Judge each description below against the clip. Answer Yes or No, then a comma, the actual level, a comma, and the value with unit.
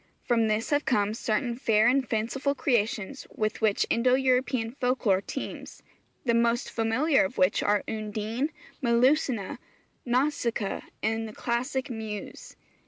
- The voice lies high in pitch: Yes, high, 235 Hz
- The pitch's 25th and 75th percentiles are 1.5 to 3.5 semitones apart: Yes, average, 3.1 semitones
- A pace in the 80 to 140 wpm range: Yes, slow, 135 wpm